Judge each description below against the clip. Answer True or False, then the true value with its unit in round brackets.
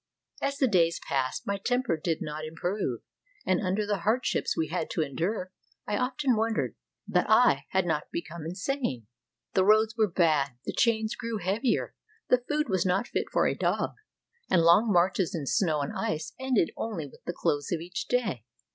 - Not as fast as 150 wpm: False (180 wpm)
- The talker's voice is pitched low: False (185 Hz)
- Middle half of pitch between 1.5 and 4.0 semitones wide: False (5.3 semitones)